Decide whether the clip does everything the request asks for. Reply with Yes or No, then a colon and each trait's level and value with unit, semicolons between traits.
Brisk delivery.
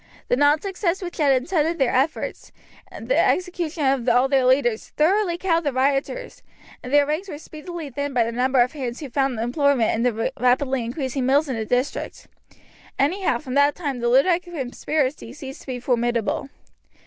No: average, 185 wpm